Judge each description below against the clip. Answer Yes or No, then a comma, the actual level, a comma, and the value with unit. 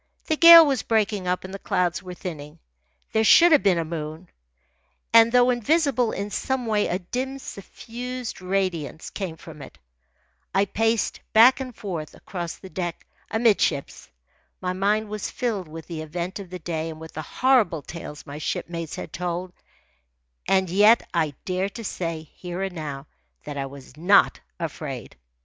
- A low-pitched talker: No, medium, 185 Hz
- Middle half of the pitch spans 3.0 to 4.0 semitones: No, wide, 5.4 semitones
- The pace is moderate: Yes, average, 165 wpm